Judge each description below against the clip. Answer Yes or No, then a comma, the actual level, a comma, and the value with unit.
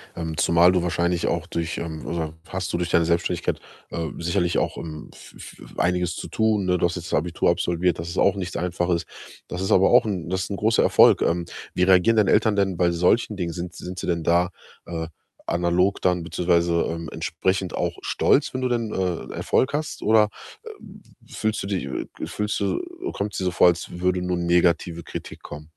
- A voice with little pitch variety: Yes, narrow, 2.0 semitones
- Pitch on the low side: Yes, very low, 90 Hz